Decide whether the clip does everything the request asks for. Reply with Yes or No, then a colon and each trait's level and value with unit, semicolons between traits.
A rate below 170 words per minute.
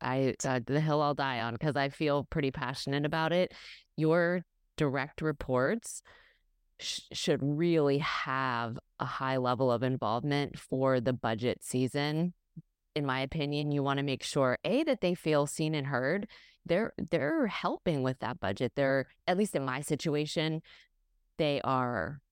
Yes: average, 160 wpm